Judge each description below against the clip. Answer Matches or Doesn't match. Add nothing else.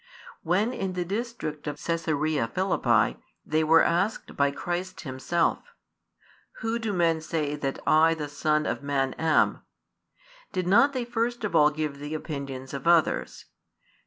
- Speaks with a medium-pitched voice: Matches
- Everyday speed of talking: Matches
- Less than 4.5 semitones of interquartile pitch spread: Matches